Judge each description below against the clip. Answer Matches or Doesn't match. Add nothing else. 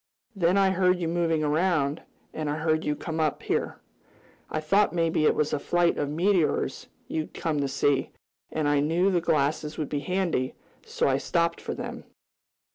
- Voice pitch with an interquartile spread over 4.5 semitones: Doesn't match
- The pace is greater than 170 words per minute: Matches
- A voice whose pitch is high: Doesn't match